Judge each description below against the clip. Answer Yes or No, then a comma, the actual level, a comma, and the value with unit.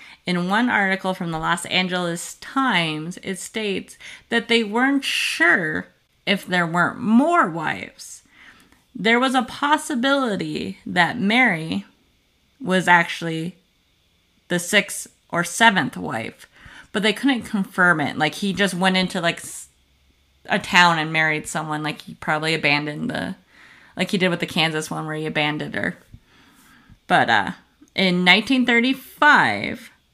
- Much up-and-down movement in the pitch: Yes, wide, 6.2 semitones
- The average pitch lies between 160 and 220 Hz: Yes, medium, 185 Hz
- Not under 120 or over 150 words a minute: Yes, slow, 135 wpm